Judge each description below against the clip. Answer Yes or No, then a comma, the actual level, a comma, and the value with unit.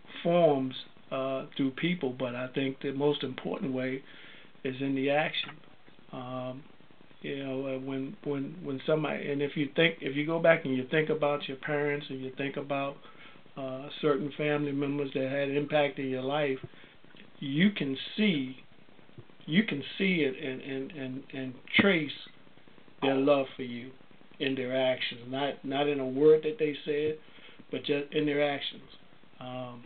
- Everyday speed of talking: Yes, average, 170 wpm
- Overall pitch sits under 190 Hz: Yes, medium, 140 Hz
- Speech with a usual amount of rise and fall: No, narrow, 2.0 semitones